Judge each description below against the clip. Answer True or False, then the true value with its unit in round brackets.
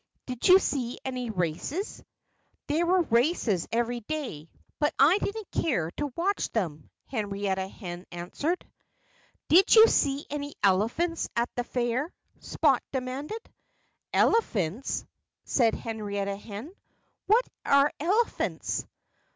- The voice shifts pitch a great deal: True (8.2 semitones)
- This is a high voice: True (255 Hz)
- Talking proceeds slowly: True (115 wpm)